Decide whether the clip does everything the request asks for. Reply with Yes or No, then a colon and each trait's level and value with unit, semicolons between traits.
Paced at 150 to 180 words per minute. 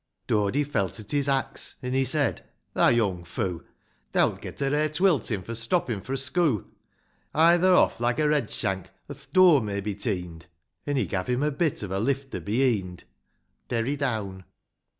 No: average, 190 wpm